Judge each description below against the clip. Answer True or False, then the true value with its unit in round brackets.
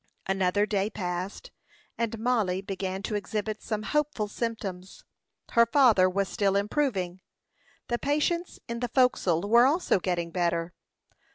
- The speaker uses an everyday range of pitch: True (4.1 semitones)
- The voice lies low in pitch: False (205 Hz)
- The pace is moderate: False (130 wpm)